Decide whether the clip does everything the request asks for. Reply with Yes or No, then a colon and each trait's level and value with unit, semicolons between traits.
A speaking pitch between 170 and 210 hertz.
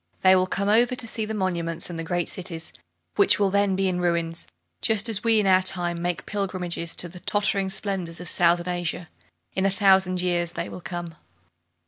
Yes: medium, 185 Hz